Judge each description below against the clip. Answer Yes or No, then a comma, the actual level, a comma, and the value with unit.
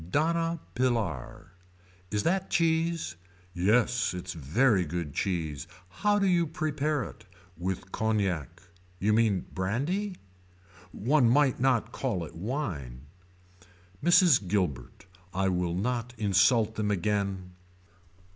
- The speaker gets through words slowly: Yes, slow, 110 wpm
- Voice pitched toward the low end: Yes, low, 105 Hz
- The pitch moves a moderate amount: No, wide, 7.6 semitones